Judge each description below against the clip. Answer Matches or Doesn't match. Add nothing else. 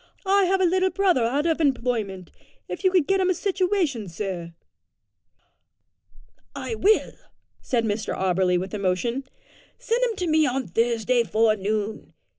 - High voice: Matches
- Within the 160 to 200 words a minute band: Doesn't match